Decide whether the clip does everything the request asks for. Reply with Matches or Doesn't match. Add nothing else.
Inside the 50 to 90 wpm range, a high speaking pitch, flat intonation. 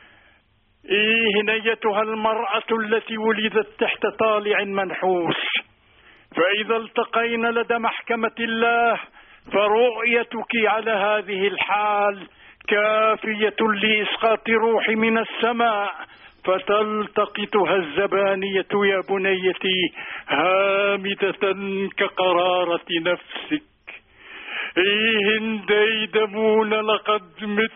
Matches